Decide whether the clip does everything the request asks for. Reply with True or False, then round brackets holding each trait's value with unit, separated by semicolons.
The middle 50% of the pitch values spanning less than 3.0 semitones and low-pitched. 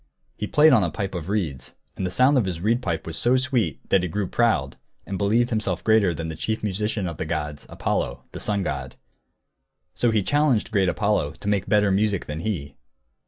False (4.6 semitones; 100 Hz)